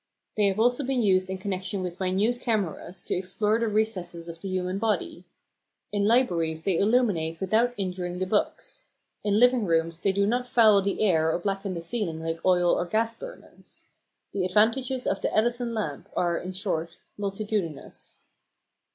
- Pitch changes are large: No, average, 3.7 semitones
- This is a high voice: Yes, high, 195 Hz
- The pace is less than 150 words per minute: No, average, 170 wpm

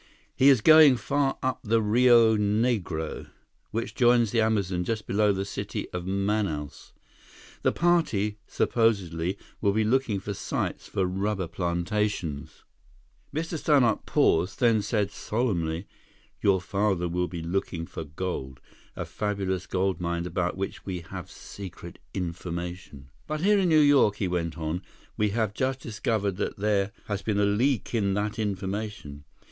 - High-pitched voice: No, low, 100 Hz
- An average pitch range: Yes, average, 3.9 semitones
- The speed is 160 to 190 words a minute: No, average, 145 wpm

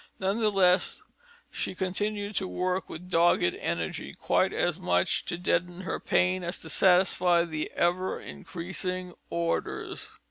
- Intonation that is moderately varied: No, narrow, 1.6 semitones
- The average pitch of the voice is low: No, medium, 180 Hz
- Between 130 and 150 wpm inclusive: Yes, average, 140 wpm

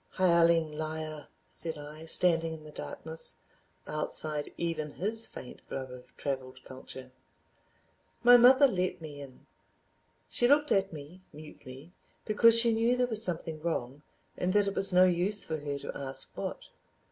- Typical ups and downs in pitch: Yes, average, 4.8 semitones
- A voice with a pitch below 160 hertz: No, medium, 165 Hz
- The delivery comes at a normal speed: Yes, average, 155 wpm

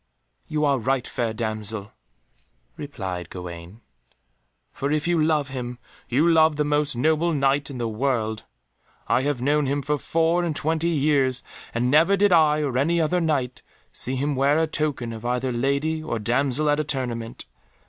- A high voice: No, medium, 140 Hz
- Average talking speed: Yes, average, 170 wpm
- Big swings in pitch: No, average, 4.0 semitones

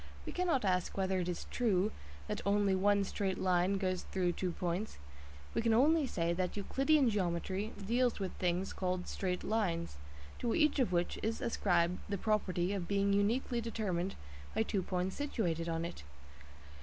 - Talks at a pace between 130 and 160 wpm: No, average, 170 wpm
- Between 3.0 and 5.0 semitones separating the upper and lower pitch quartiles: Yes, average, 3.6 semitones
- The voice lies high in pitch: Yes, high, 195 Hz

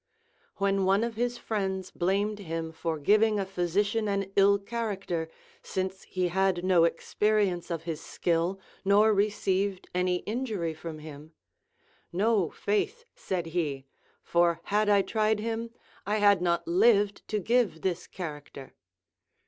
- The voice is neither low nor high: No, high, 195 Hz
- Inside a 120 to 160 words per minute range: Yes, average, 140 wpm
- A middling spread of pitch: Yes, average, 3.4 semitones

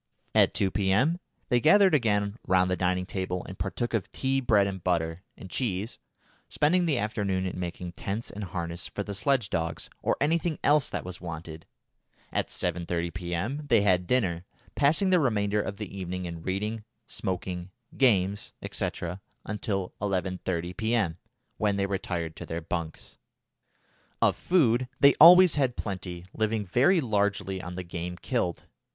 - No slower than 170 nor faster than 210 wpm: No, average, 160 wpm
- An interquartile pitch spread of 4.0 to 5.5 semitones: Yes, average, 5.0 semitones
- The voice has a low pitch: Yes, low, 100 Hz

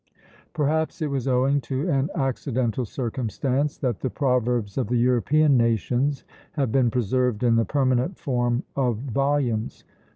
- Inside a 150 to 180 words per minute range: No, average, 140 wpm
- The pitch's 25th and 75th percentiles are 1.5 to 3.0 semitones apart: Yes, narrow, 2.6 semitones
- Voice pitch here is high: No, low, 130 Hz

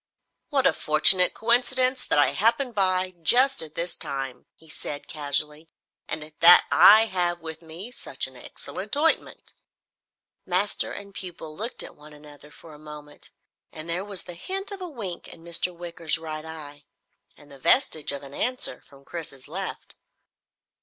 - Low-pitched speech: No, medium, 170 Hz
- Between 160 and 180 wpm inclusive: Yes, average, 165 wpm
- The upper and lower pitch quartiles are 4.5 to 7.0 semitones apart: Yes, wide, 5.4 semitones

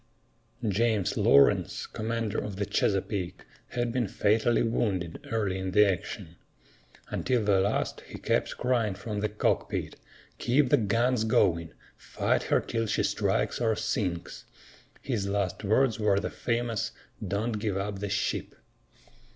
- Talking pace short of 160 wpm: Yes, average, 140 wpm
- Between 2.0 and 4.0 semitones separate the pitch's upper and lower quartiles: Yes, average, 2.8 semitones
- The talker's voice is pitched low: Yes, low, 105 Hz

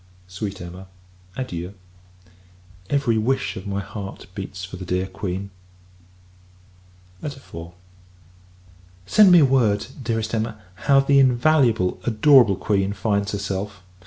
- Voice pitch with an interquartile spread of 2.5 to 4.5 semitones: No, average, 5.0 semitones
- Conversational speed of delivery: No, slow, 110 wpm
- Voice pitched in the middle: No, low, 105 Hz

